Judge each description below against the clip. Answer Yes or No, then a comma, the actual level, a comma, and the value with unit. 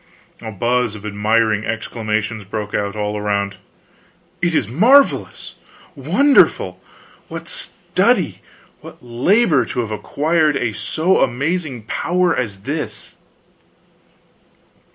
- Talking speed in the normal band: No, slow, 105 wpm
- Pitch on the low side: Yes, low, 115 Hz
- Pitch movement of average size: No, wide, 6.8 semitones